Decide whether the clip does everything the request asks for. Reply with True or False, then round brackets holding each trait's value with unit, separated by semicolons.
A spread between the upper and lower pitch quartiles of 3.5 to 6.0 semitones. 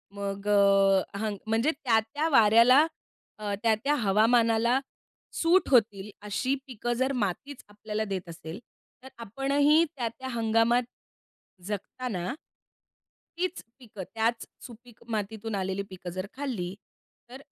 True (4.2 semitones)